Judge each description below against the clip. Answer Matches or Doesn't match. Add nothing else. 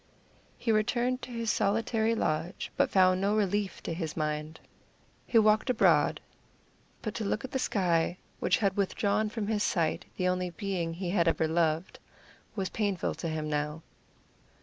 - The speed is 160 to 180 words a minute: Matches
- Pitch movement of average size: Matches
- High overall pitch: Matches